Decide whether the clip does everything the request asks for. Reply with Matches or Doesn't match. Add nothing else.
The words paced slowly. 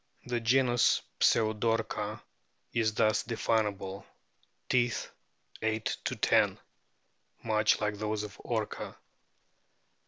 Matches